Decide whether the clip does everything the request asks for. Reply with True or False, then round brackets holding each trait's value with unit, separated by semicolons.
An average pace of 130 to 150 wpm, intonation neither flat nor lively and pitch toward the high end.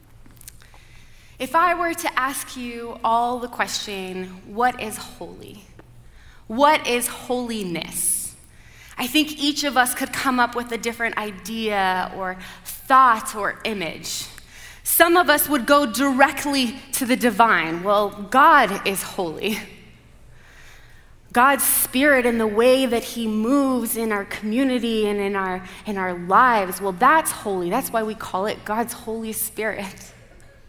True (140 wpm; 4.4 semitones; 235 Hz)